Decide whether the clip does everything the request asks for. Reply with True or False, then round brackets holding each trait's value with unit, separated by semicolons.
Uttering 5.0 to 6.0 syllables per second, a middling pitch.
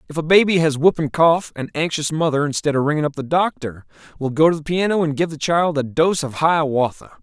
True (5.8 syllables/s; 155 Hz)